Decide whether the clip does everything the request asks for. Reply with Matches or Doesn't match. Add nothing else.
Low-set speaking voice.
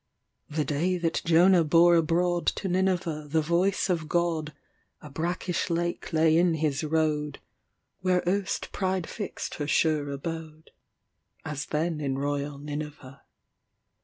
Doesn't match